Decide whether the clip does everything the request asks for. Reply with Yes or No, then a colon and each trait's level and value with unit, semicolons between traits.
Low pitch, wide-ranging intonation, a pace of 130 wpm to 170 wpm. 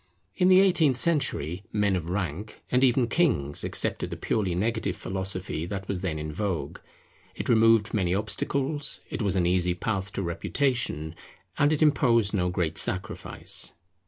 Yes: low, 100 Hz; wide, 5.9 semitones; average, 160 wpm